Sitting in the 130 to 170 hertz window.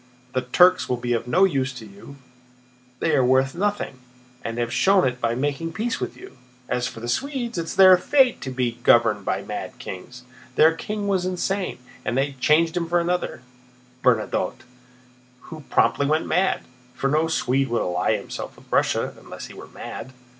Yes: low, 135 Hz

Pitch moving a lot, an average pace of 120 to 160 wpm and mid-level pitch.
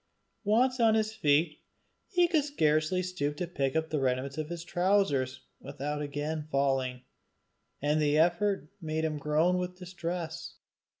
No: average, 3.8 semitones; average, 140 wpm; medium, 160 Hz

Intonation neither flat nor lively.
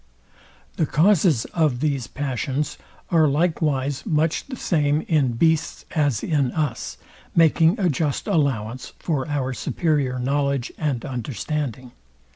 Yes: average, 3.4 semitones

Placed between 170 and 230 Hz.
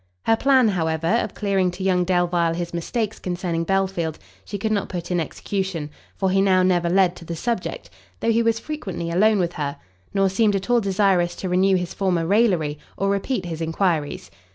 Yes: medium, 185 Hz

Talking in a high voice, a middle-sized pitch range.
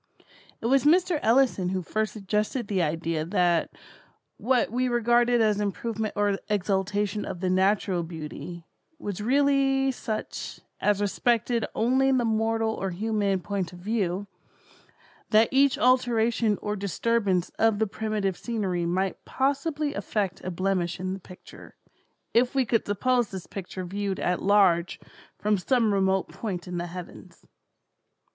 Yes: high, 210 Hz; average, 4.1 semitones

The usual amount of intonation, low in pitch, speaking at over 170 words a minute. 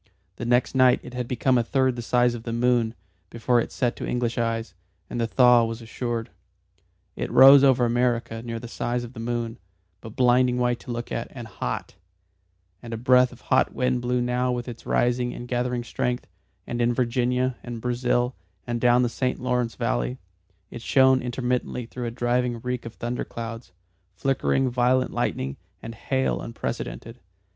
No: narrow, 1.2 semitones; low, 120 Hz; average, 180 wpm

